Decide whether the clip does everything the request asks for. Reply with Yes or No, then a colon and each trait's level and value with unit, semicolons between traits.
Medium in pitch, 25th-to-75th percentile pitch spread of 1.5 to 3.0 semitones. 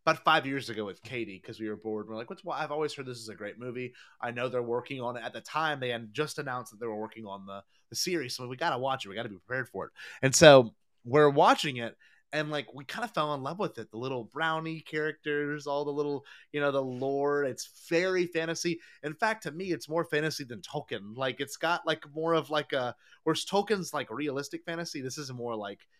No: medium, 145 Hz; average, 4.5 semitones